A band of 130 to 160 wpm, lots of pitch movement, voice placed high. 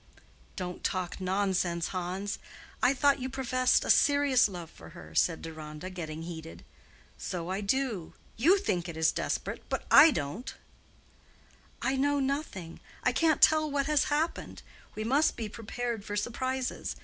Yes: average, 150 wpm; wide, 7.6 semitones; high, 210 Hz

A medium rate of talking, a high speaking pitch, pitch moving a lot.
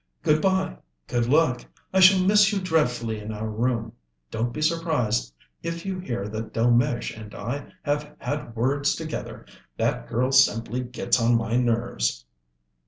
No: average, 155 wpm; low, 125 Hz; wide, 5.7 semitones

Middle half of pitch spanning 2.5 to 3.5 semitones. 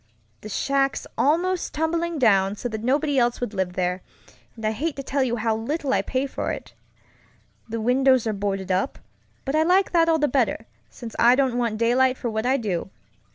No: average, 4.4 semitones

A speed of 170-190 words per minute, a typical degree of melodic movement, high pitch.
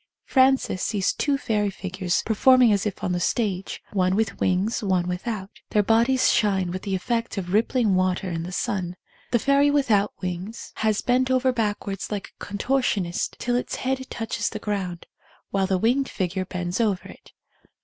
Yes: average, 175 wpm; average, 4.2 semitones; high, 205 Hz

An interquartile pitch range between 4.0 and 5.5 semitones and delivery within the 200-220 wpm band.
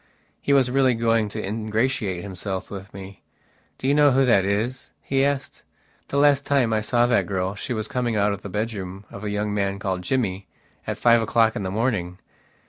Yes: average, 4.3 semitones; fast, 205 wpm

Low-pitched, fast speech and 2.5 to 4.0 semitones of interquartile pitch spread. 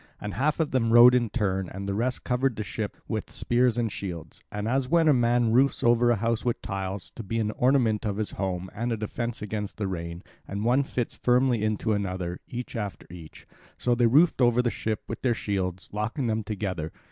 Yes: low, 110 Hz; fast, 215 wpm; average, 3.6 semitones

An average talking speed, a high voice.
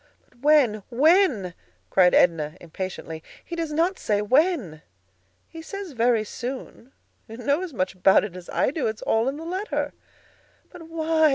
Yes: average, 170 wpm; very high, 255 Hz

